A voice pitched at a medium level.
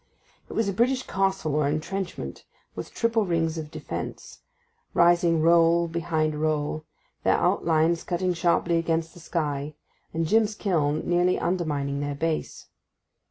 Yes: medium, 165 Hz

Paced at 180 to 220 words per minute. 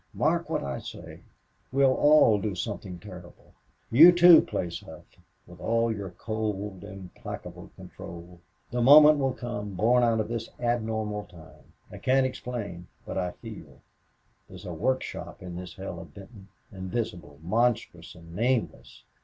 No: average, 150 wpm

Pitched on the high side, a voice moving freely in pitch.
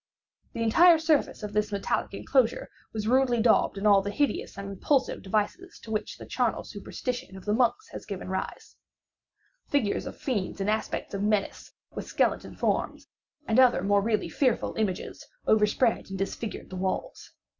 No: high, 215 Hz; average, 4.0 semitones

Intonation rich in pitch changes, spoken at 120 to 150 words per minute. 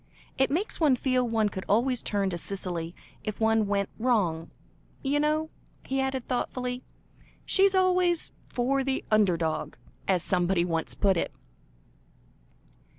Yes: wide, 6.0 semitones; average, 140 wpm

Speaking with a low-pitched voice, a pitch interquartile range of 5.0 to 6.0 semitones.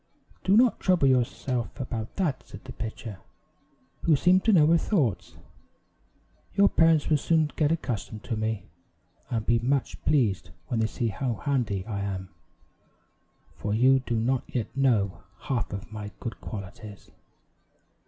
Yes: low, 120 Hz; average, 5.3 semitones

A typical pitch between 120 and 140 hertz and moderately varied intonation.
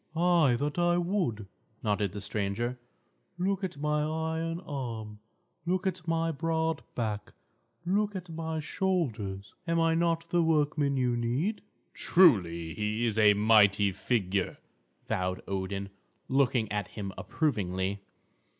No: low, 135 Hz; wide, 8.0 semitones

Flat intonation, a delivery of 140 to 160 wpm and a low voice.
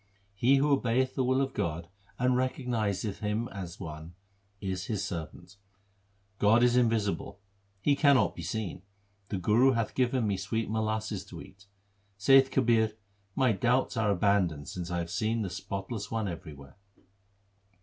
No: average, 4.6 semitones; average, 155 wpm; low, 110 Hz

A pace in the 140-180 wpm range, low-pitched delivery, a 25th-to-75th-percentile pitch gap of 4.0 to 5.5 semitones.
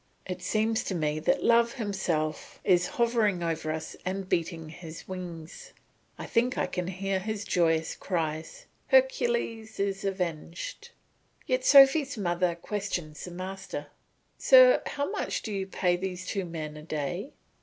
No: average, 145 wpm; medium, 185 Hz; average, 4.7 semitones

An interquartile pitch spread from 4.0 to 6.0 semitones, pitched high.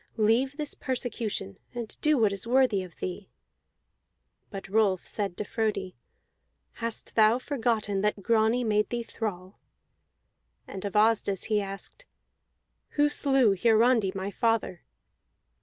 No: average, 3.3 semitones; high, 220 Hz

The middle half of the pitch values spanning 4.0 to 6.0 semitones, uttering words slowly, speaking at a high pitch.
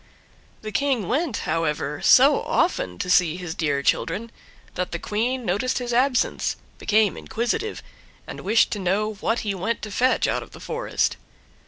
No: average, 5.2 semitones; average, 165 wpm; high, 215 Hz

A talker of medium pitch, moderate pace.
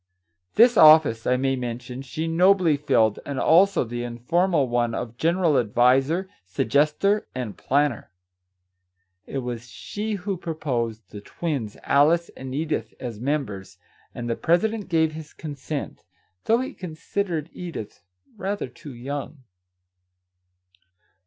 No: medium, 145 Hz; slow, 125 wpm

